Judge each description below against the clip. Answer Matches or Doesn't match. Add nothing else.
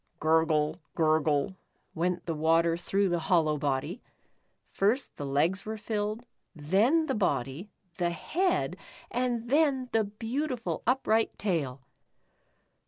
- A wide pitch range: Matches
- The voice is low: Doesn't match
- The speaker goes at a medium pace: Doesn't match